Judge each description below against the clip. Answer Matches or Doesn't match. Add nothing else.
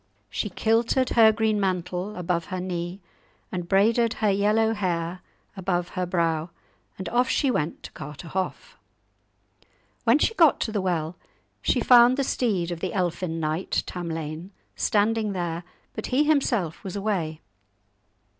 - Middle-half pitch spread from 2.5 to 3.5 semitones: Doesn't match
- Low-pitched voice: Doesn't match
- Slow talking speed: Doesn't match